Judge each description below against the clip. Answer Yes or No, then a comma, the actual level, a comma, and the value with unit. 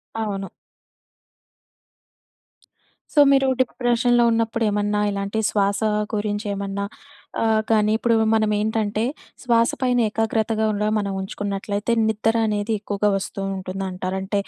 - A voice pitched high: Yes, high, 210 Hz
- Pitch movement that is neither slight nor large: No, narrow, 1.9 semitones